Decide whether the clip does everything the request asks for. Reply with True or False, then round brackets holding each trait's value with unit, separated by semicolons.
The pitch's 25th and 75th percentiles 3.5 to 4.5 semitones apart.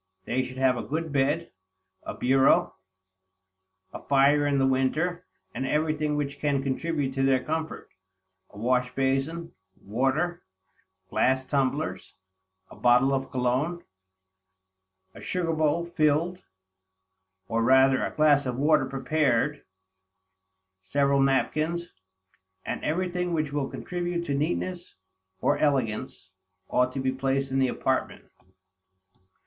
False (3.1 semitones)